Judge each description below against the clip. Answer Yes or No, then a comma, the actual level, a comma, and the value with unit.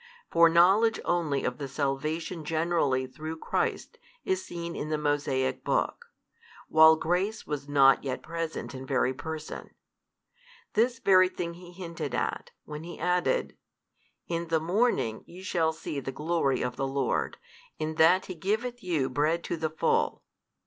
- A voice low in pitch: No, medium, 160 Hz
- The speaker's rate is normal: Yes, average, 155 wpm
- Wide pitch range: No, average, 3.5 semitones